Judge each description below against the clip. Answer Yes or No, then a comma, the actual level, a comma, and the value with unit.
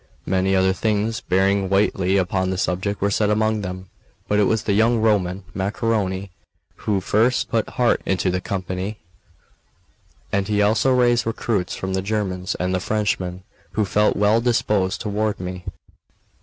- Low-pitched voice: Yes, low, 100 Hz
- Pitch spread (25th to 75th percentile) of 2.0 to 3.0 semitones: Yes, narrow, 2.5 semitones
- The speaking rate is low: No, average, 155 wpm